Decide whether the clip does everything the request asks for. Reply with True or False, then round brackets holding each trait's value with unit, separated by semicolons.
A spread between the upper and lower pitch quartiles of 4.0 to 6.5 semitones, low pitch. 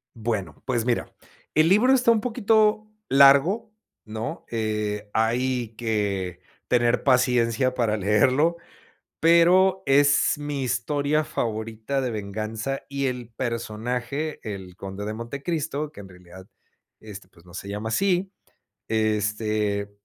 True (5.1 semitones; 120 Hz)